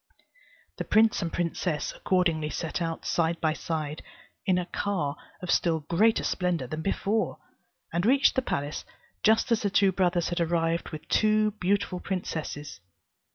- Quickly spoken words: No, average, 155 wpm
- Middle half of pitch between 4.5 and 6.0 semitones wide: No, average, 3.8 semitones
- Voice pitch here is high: No, medium, 175 Hz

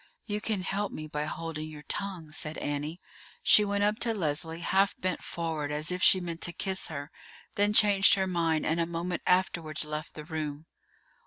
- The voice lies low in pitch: No, medium, 170 Hz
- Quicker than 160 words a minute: Yes, average, 190 wpm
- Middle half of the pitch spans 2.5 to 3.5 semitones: No, average, 3.9 semitones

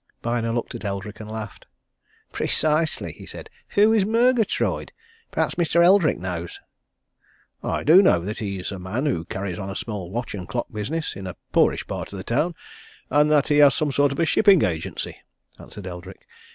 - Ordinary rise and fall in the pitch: No, wide, 8.3 semitones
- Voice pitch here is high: No, low, 120 Hz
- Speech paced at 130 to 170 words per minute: No, average, 190 wpm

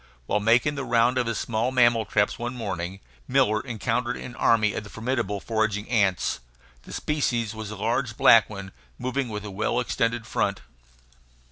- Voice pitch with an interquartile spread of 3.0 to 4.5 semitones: No, narrow, 2.6 semitones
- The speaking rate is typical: Yes, average, 170 wpm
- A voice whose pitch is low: Yes, low, 115 Hz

